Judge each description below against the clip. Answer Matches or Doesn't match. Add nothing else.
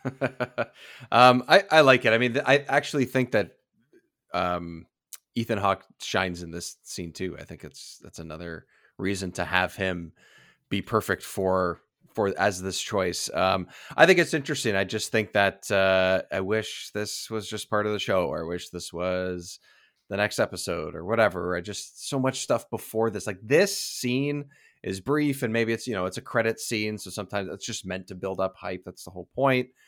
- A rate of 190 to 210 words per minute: Matches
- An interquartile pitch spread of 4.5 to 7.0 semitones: Matches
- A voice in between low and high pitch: Doesn't match